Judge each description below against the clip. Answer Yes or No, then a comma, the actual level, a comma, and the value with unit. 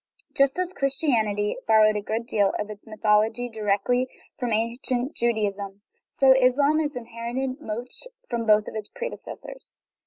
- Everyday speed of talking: Yes, average, 145 wpm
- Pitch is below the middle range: No, high, 235 Hz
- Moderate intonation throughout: Yes, average, 3.7 semitones